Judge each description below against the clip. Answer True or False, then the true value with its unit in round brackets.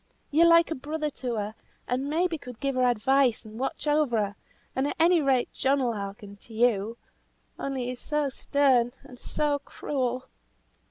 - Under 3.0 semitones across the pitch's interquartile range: False (3.6 semitones)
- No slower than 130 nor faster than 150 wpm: False (175 wpm)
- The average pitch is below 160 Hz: False (260 Hz)